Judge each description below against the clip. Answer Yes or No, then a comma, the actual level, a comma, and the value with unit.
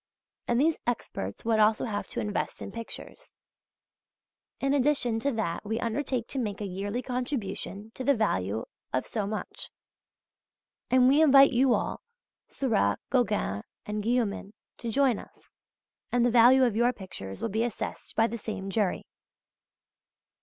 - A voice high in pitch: Yes, high, 230 Hz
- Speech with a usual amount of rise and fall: Yes, average, 3.6 semitones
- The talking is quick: No, average, 155 wpm